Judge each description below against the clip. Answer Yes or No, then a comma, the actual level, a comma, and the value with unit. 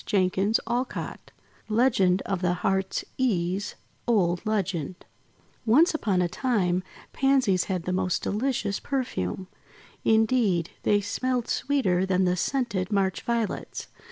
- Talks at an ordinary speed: No, slow, 120 wpm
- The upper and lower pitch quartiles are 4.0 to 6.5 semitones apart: Yes, average, 4.6 semitones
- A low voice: No, high, 195 Hz